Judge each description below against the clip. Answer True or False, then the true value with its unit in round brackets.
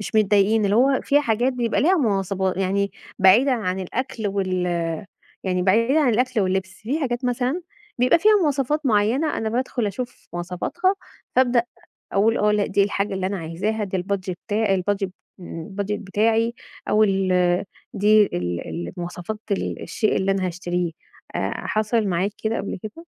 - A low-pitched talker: False (210 Hz)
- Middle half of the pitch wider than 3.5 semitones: True (4.1 semitones)